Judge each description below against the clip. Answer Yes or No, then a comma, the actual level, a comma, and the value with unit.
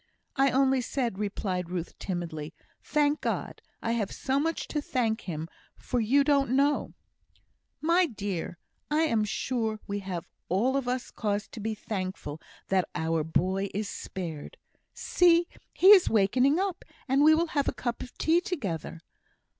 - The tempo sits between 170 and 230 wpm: No, average, 160 wpm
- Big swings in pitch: Yes, wide, 7.0 semitones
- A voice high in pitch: Yes, high, 230 Hz